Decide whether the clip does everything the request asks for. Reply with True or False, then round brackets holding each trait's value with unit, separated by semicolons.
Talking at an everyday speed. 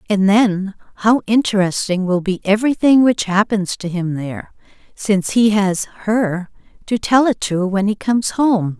True (165 wpm)